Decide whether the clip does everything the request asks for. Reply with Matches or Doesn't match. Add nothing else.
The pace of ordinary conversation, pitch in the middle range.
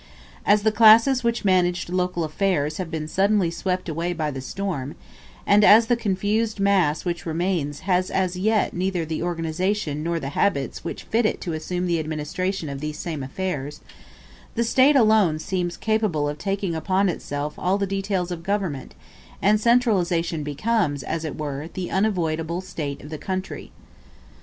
Matches